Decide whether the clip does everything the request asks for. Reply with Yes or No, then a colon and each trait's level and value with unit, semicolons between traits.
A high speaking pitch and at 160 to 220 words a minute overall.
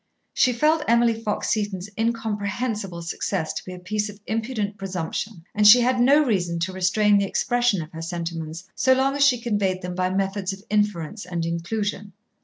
Yes: high, 205 Hz; average, 185 wpm